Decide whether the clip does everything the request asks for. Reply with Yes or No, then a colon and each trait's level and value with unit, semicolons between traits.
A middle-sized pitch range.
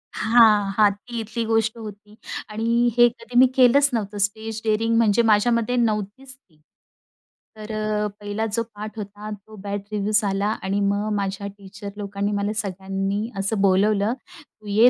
No: narrow, 2.0 semitones